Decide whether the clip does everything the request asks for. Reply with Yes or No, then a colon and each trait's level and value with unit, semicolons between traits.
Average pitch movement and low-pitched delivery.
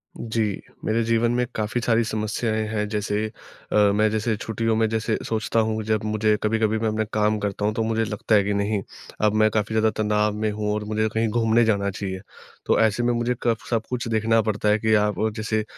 No: narrow, 1.1 semitones; low, 110 Hz